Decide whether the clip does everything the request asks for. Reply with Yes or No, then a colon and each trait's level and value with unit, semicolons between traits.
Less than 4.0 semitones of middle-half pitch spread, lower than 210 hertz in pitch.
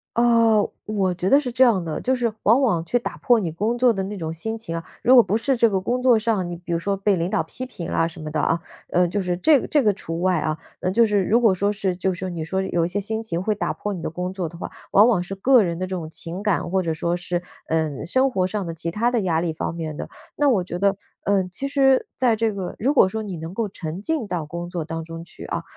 No: average, 4.8 semitones; high, 190 Hz